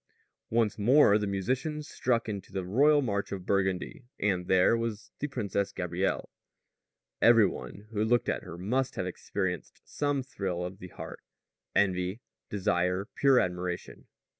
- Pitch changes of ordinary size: Yes, average, 4.6 semitones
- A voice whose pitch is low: Yes, low, 100 Hz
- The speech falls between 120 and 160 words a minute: Yes, average, 145 wpm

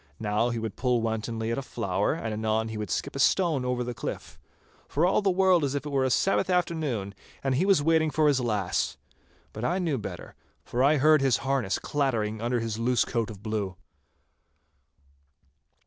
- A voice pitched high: No, low, 125 Hz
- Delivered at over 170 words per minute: Yes, average, 195 wpm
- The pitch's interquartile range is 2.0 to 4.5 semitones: No, average, 5.0 semitones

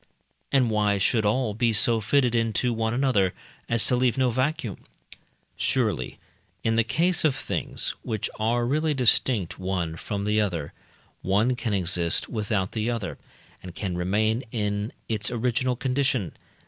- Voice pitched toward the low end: Yes, low, 110 Hz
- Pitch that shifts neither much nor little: Yes, average, 3.5 semitones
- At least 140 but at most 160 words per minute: Yes, average, 150 wpm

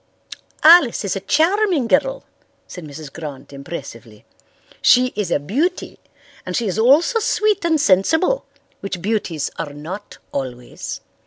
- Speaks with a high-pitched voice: Yes, high, 205 Hz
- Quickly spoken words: No, slow, 135 wpm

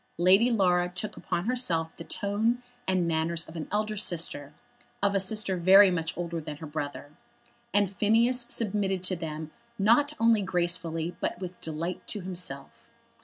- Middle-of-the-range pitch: Yes, medium, 180 Hz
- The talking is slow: No, average, 160 wpm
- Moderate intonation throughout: Yes, average, 3.8 semitones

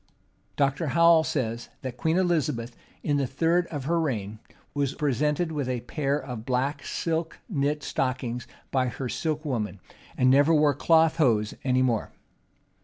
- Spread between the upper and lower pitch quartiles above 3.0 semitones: Yes, average, 4.0 semitones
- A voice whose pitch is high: No, medium, 140 Hz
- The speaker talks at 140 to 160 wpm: Yes, average, 155 wpm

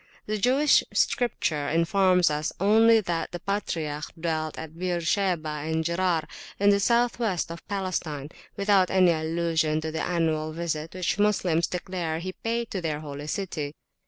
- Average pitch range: Yes, average, 3.8 semitones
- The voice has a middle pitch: Yes, medium, 170 Hz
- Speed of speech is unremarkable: Yes, average, 155 wpm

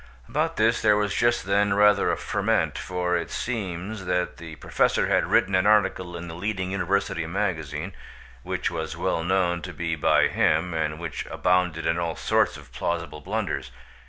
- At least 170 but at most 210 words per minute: Yes, average, 175 wpm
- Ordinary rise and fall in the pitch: Yes, average, 3.0 semitones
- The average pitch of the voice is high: No, very low, 90 Hz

